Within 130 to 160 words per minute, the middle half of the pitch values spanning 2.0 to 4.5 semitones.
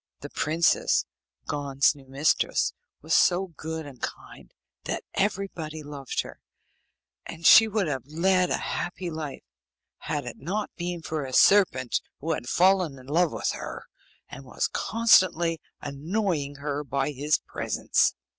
Yes: average, 145 wpm; average, 4.1 semitones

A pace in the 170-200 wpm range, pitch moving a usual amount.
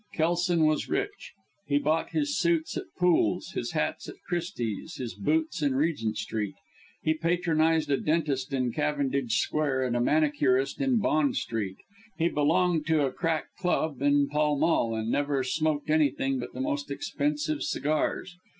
No: average, 160 wpm; average, 3.8 semitones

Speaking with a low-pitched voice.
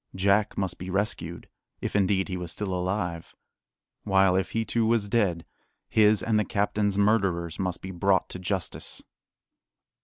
Yes: very low, 95 Hz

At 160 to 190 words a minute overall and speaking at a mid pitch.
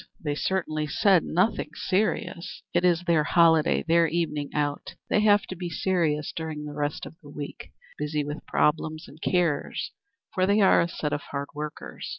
Yes: average, 175 wpm; medium, 160 Hz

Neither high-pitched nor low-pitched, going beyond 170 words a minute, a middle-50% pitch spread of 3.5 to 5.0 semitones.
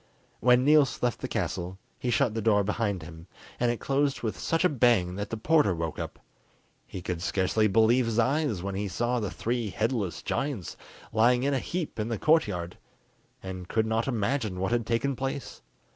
No: low, 115 Hz; average, 190 wpm; average, 4.7 semitones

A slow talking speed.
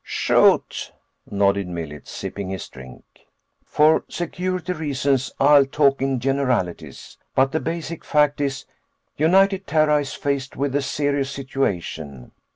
Yes: slow, 125 wpm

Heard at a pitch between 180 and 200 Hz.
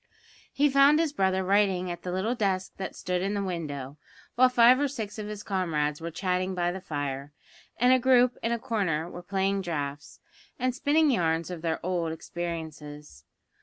Yes: medium, 185 Hz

